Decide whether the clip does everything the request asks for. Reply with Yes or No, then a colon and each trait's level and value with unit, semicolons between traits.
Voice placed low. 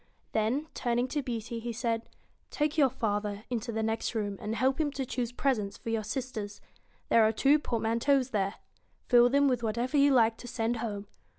No: high, 235 Hz